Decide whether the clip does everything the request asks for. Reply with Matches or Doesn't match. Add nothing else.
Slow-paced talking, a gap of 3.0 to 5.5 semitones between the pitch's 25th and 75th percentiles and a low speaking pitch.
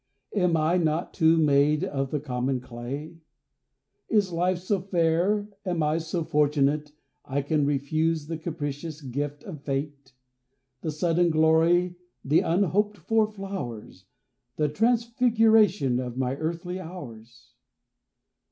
Doesn't match